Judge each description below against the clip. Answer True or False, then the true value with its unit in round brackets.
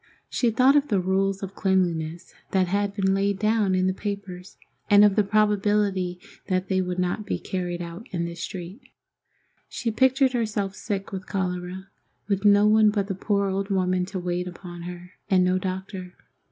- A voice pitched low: False (195 Hz)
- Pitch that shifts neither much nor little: False (2.2 semitones)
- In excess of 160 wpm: True (180 wpm)